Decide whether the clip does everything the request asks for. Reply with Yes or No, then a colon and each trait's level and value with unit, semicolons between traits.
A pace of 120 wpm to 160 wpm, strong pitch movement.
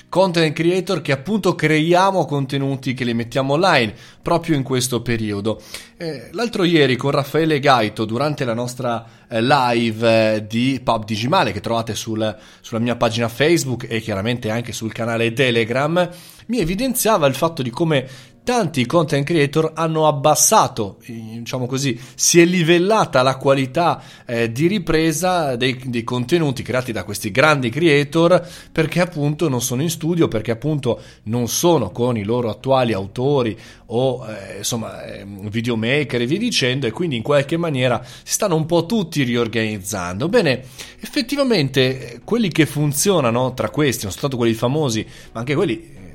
Yes: average, 150 wpm; wide, 5.9 semitones